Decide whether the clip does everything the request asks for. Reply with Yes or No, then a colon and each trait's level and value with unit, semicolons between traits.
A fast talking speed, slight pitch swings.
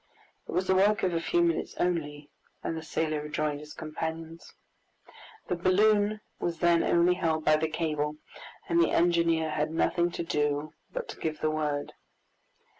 No: average, 170 wpm; narrow, 2.2 semitones